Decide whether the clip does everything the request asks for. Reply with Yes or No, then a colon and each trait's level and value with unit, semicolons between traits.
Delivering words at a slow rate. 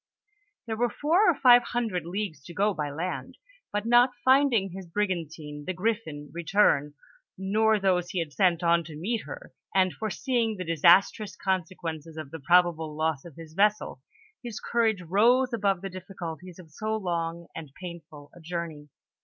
No: average, 170 wpm